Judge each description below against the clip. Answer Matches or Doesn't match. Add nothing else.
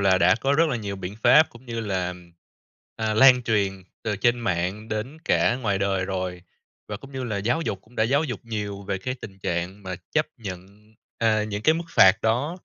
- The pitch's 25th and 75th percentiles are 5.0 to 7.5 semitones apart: Doesn't match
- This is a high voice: Doesn't match